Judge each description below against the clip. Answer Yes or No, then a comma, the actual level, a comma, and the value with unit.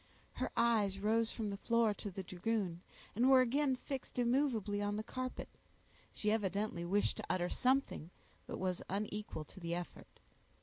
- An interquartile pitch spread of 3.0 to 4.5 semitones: Yes, average, 3.7 semitones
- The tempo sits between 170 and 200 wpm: No, average, 160 wpm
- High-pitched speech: Yes, high, 210 Hz